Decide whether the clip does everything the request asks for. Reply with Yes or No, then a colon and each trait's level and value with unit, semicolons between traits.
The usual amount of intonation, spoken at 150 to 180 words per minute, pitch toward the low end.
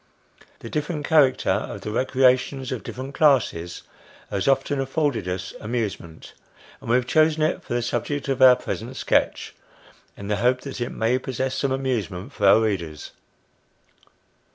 Yes: average, 4.1 semitones; average, 155 wpm; low, 125 Hz